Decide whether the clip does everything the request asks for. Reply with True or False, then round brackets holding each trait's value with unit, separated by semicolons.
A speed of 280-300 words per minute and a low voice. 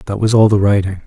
True (285 wpm; 100 Hz)